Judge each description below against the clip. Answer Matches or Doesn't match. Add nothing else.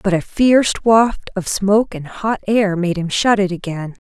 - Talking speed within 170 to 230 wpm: Matches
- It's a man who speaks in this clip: Doesn't match